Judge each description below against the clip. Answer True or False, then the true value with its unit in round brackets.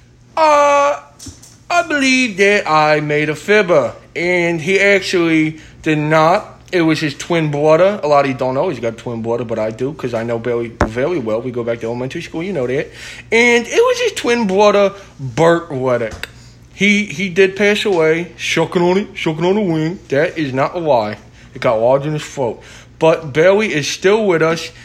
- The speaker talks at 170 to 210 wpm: True (205 wpm)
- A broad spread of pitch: True (6.1 semitones)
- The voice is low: False (165 Hz)